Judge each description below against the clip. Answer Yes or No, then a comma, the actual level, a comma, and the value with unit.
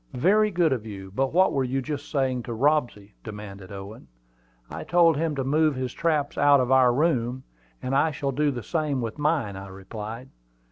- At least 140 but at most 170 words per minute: No, average, 195 wpm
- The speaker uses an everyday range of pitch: Yes, average, 4.9 semitones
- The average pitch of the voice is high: No, low, 130 Hz